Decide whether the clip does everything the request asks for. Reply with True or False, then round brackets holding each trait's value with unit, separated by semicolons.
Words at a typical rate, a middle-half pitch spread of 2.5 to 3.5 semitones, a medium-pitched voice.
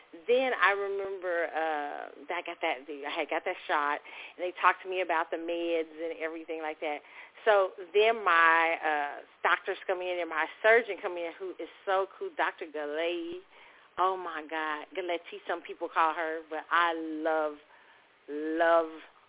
True (175 wpm; 2.8 semitones; 170 Hz)